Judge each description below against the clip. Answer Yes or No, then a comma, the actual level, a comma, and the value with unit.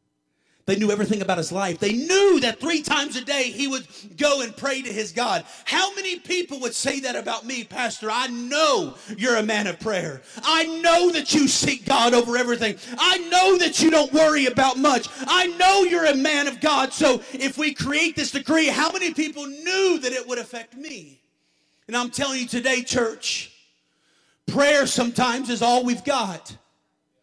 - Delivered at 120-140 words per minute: No, average, 190 wpm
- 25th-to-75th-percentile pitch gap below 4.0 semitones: No, average, 4.5 semitones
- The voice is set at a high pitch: Yes, very high, 265 Hz